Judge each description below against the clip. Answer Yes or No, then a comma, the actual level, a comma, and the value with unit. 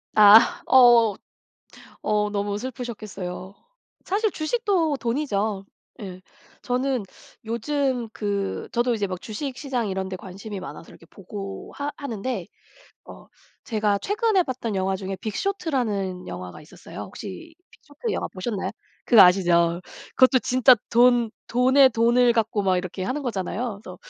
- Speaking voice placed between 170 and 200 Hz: No, high, 225 Hz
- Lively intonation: No, average, 4.9 semitones